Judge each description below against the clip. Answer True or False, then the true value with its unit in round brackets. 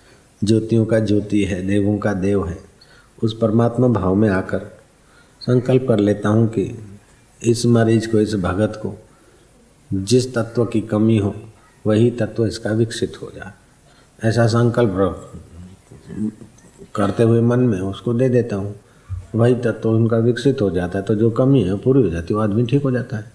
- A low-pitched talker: True (110 Hz)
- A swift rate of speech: False (170 wpm)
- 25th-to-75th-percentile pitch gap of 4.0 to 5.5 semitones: False (2.8 semitones)